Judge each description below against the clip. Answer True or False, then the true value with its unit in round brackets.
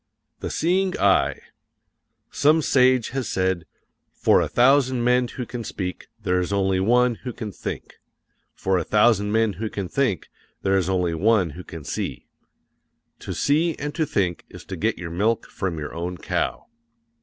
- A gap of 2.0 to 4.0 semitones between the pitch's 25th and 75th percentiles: False (5.4 semitones)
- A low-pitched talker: True (105 Hz)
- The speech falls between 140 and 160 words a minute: False (170 wpm)